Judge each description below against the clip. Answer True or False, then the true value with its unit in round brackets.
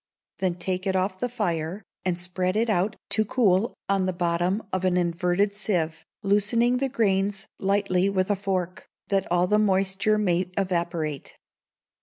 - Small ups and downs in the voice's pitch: True (2.3 semitones)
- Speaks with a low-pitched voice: False (190 Hz)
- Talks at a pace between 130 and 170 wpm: True (160 wpm)